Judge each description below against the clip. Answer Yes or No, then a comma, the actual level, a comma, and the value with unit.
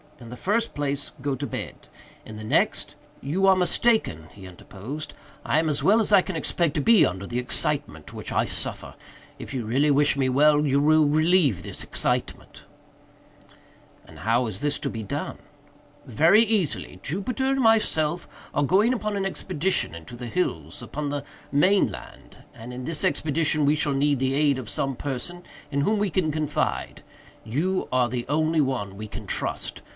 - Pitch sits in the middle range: Yes, medium, 145 Hz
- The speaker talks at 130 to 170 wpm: No, average, 180 wpm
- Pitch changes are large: Yes, wide, 6.0 semitones